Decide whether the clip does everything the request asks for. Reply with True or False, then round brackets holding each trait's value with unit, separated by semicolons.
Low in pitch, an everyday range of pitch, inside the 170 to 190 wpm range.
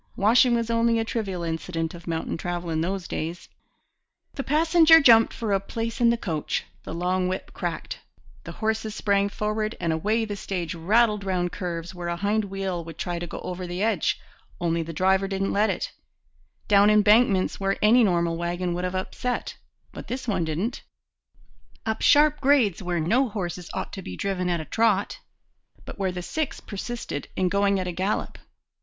False (195 Hz; 4.1 semitones; 185 wpm)